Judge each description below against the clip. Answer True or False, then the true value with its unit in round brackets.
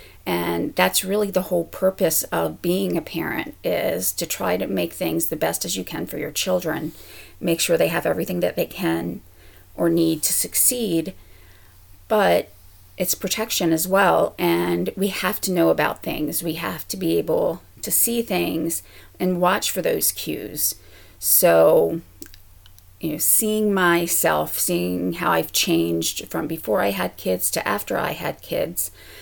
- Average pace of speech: True (165 wpm)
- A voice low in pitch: False (160 Hz)